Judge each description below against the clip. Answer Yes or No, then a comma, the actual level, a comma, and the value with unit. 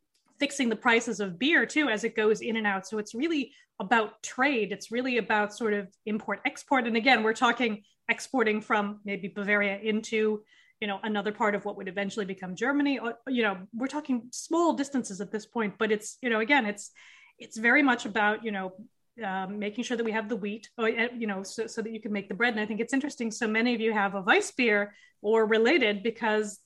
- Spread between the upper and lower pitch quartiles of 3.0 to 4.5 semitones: No, narrow, 2.6 semitones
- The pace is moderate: No, fast, 225 wpm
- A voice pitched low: No, high, 225 Hz